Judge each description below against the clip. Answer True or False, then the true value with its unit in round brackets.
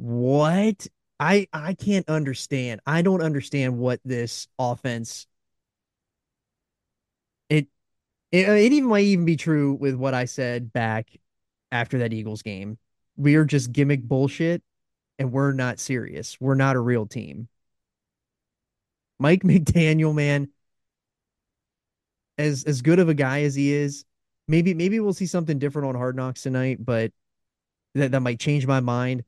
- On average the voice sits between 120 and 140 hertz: True (135 Hz)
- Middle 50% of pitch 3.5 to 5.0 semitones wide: True (4.3 semitones)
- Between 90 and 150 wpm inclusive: True (145 wpm)